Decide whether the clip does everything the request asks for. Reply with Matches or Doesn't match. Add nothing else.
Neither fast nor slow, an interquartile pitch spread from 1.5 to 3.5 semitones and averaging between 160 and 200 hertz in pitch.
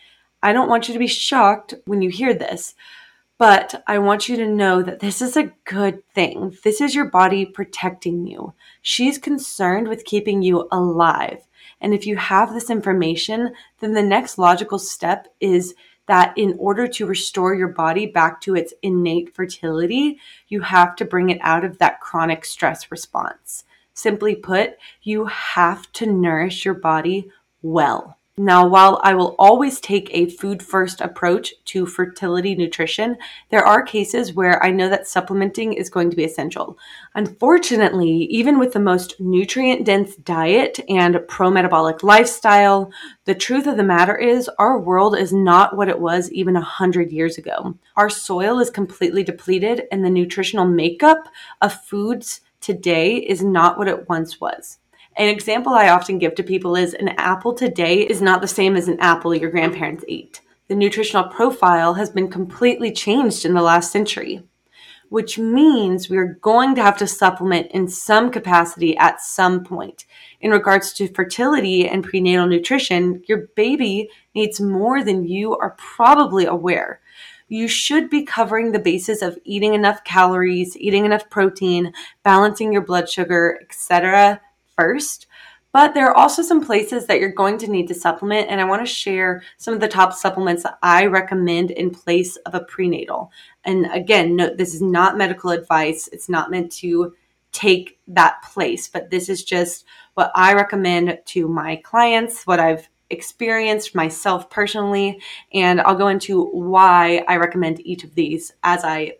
Matches